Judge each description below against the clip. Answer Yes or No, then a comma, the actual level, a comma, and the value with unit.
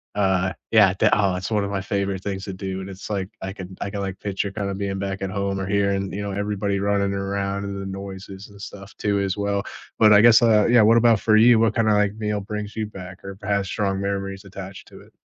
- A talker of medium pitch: No, low, 100 Hz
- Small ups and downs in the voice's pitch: Yes, narrow, 1.1 semitones